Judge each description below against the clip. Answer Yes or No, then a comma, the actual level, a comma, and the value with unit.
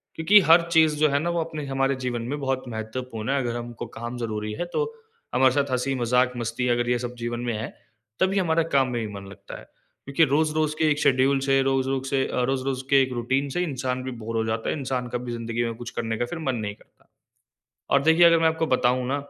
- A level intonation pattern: No, average, 3.2 semitones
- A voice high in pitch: No, low, 130 Hz